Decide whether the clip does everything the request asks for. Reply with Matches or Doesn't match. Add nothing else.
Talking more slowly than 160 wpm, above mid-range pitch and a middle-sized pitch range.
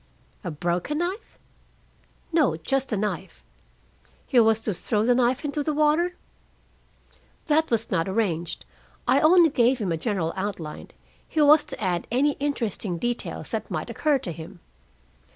Doesn't match